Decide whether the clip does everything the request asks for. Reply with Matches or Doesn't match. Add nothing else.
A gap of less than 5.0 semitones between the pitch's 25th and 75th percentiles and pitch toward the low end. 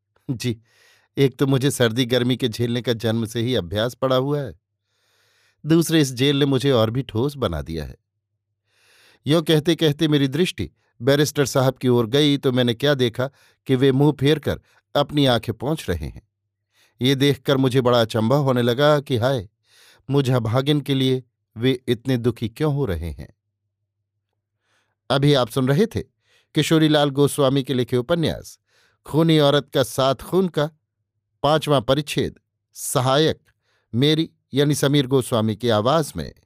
Matches